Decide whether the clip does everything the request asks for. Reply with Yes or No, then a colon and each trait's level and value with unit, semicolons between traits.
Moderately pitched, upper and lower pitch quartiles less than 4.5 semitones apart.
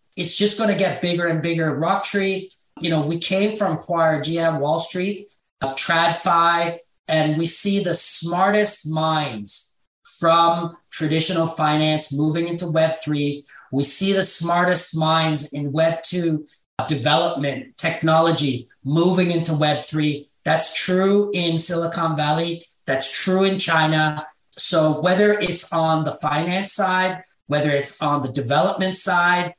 Yes: medium, 165 Hz; average, 2.8 semitones